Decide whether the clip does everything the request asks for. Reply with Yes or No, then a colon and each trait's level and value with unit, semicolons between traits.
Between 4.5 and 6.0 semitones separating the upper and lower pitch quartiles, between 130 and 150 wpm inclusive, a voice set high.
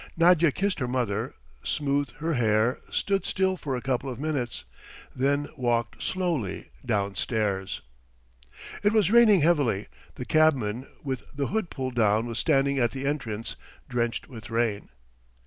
No: average, 5.2 semitones; average, 145 wpm; low, 130 Hz